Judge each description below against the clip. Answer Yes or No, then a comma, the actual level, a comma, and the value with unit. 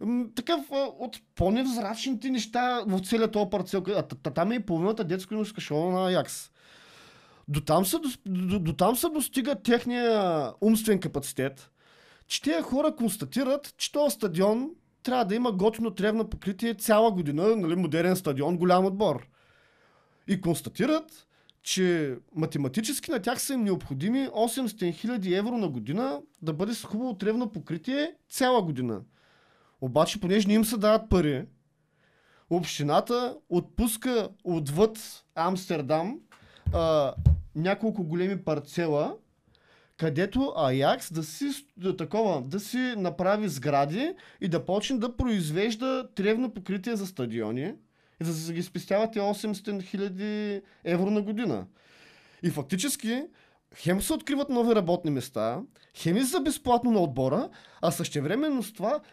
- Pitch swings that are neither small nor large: No, wide, 6.2 semitones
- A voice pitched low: No, high, 200 Hz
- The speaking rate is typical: Yes, average, 130 wpm